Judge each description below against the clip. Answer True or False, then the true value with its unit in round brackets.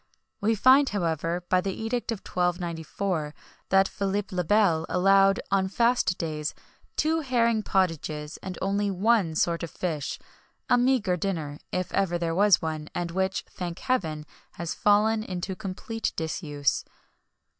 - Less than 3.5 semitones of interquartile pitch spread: False (3.8 semitones)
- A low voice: False (185 Hz)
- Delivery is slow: False (145 wpm)